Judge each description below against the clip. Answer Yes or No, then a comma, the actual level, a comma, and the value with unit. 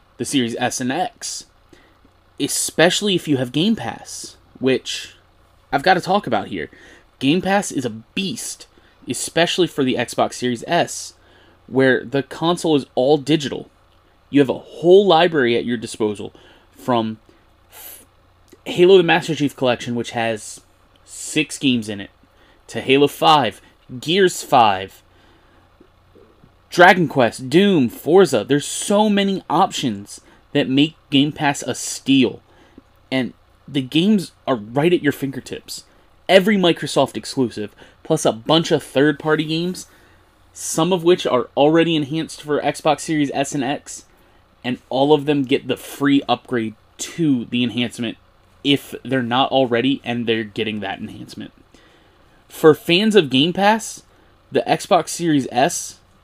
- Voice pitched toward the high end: No, low, 135 Hz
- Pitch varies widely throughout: Yes, wide, 5.7 semitones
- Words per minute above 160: No, average, 145 wpm